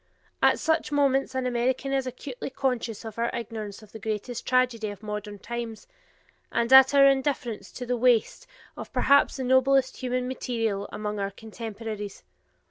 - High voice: Yes, high, 240 Hz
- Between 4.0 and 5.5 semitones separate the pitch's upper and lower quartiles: No, average, 3.2 semitones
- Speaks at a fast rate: No, average, 160 wpm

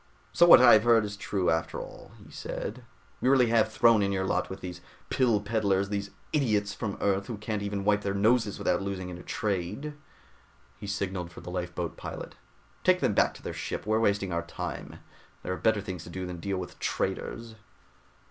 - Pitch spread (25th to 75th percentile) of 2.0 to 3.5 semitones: Yes, average, 2.9 semitones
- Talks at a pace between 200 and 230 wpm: Yes, fast, 205 wpm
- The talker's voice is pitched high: No, low, 100 Hz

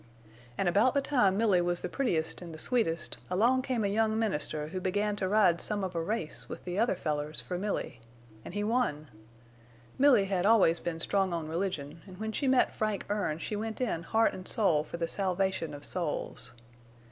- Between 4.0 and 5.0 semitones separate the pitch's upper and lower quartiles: Yes, average, 4.6 semitones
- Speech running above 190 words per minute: Yes, average, 200 wpm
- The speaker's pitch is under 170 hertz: No, high, 190 Hz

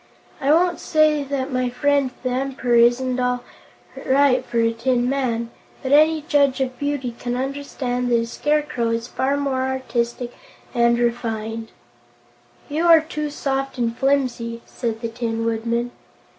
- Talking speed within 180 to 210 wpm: No, average, 150 wpm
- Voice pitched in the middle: No, very high, 255 Hz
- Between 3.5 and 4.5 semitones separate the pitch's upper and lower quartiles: No, average, 3.0 semitones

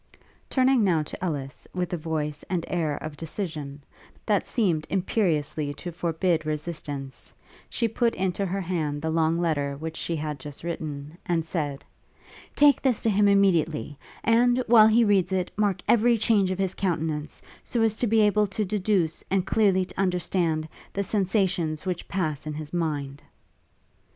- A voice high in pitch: No, medium, 175 Hz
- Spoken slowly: No, average, 165 wpm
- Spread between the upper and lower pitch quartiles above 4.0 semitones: Yes, average, 4.5 semitones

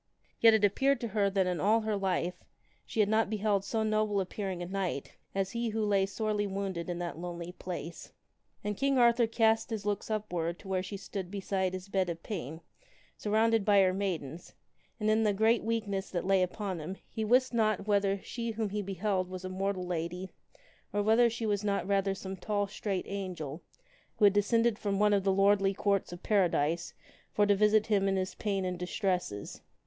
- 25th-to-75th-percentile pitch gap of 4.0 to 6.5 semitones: No, narrow, 2.4 semitones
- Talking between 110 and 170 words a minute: No, average, 200 wpm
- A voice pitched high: Yes, high, 200 Hz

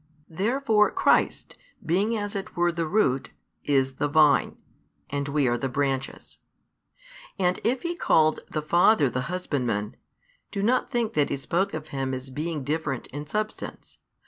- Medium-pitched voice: Yes, medium, 155 Hz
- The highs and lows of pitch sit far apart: Yes, wide, 6.5 semitones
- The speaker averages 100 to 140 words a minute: No, average, 155 wpm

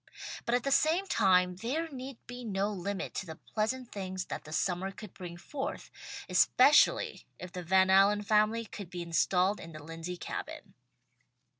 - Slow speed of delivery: No, average, 170 wpm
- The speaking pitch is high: Yes, high, 195 Hz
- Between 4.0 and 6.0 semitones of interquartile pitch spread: Yes, average, 4.3 semitones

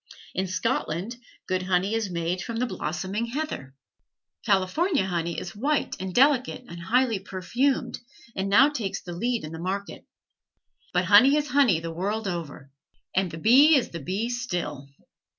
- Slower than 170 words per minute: Yes, average, 160 wpm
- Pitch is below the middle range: No, high, 195 Hz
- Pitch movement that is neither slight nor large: No, wide, 5.7 semitones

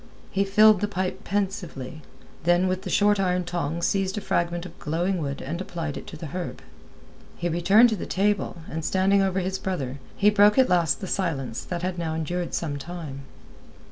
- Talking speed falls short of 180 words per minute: No, average, 195 wpm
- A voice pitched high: No, medium, 180 Hz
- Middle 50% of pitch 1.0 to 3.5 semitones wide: Yes, average, 3.1 semitones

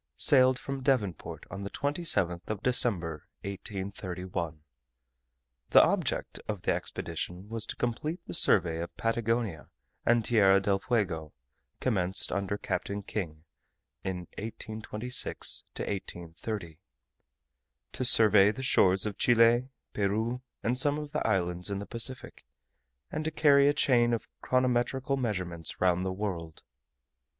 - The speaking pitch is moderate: No, low, 105 Hz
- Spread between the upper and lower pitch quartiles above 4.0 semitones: Yes, average, 5.0 semitones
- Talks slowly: Yes, slow, 125 wpm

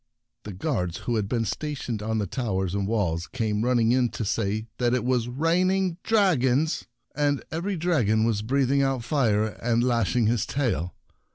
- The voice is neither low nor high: No, low, 120 Hz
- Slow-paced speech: No, average, 180 wpm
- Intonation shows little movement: No, average, 4.5 semitones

